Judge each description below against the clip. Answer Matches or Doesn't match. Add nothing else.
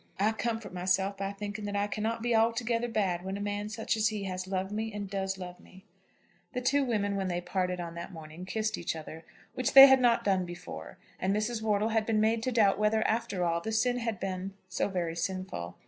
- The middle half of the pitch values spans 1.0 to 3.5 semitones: Matches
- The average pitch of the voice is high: Matches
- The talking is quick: Matches